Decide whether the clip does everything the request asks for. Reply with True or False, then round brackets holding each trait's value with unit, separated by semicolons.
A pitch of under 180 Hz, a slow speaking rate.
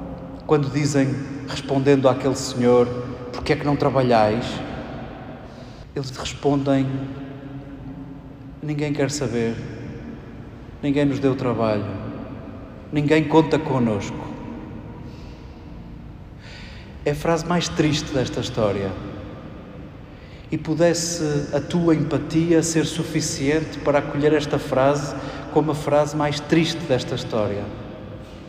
True (135 Hz; 100 wpm)